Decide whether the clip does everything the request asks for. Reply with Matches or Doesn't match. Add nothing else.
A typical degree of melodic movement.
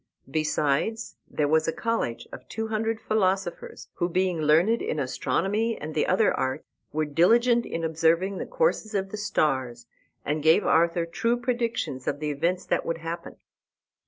Doesn't match